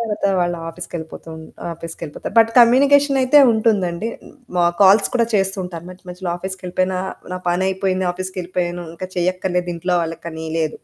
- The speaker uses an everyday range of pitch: No, narrow, 2.3 semitones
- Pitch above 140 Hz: Yes, medium, 185 Hz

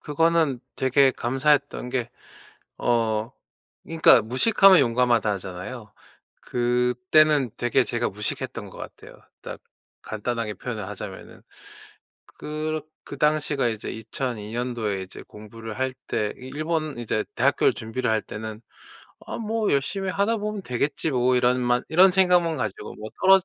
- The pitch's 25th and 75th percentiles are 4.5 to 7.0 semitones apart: Yes, wide, 5.5 semitones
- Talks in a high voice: No, low, 125 Hz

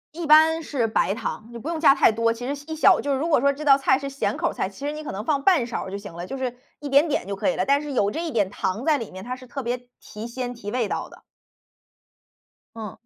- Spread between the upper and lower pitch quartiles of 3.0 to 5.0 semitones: Yes, average, 4.5 semitones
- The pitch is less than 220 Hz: No, very high, 260 Hz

